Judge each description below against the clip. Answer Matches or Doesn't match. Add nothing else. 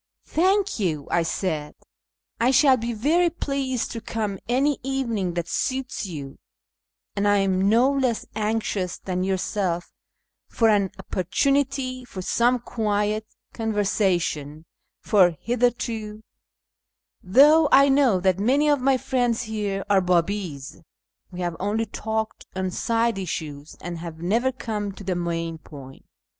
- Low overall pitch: Doesn't match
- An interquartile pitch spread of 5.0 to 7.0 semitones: Matches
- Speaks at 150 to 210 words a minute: Doesn't match